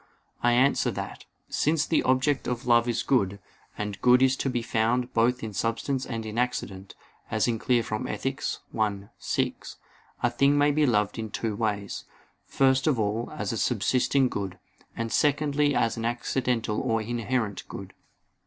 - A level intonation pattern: No, average, 3.2 semitones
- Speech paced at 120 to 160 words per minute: No, average, 170 wpm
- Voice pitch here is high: No, low, 120 Hz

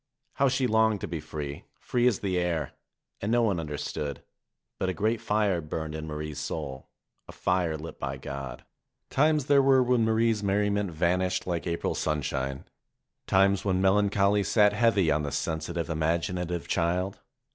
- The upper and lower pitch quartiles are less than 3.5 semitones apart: No, average, 5.0 semitones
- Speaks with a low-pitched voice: Yes, very low, 90 Hz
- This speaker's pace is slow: No, average, 160 wpm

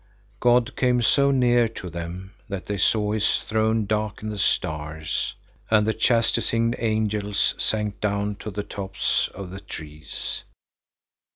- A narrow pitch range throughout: Yes, narrow, 2.3 semitones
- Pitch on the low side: Yes, low, 105 Hz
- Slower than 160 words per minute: Yes, slow, 135 wpm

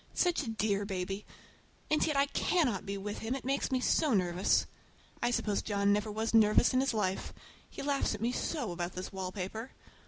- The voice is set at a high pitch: Yes, high, 215 Hz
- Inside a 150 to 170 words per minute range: No, average, 195 wpm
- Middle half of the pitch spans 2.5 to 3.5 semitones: No, average, 4.8 semitones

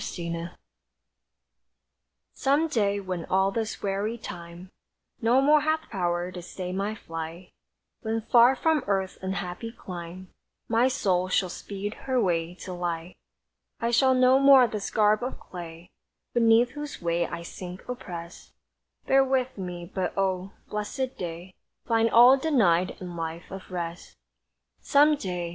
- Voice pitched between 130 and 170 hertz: No, high, 195 Hz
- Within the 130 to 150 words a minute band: Yes, average, 145 wpm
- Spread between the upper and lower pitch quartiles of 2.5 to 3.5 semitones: No, average, 5.3 semitones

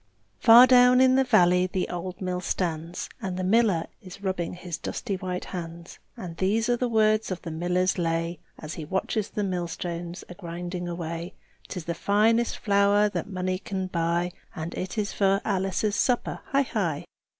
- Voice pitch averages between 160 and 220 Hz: Yes, medium, 185 Hz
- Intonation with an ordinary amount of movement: Yes, average, 3.1 semitones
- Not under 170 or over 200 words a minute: Yes, average, 175 wpm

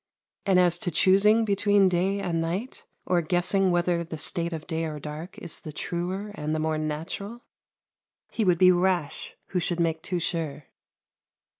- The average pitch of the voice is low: No, medium, 175 Hz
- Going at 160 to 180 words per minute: Yes, average, 170 wpm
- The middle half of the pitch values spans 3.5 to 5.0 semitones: No, average, 2.9 semitones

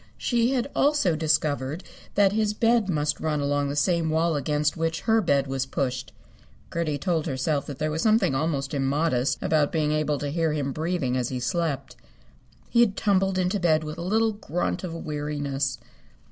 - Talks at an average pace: Yes, average, 180 wpm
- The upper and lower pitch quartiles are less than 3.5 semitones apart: No, average, 4.1 semitones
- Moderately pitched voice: Yes, medium, 155 Hz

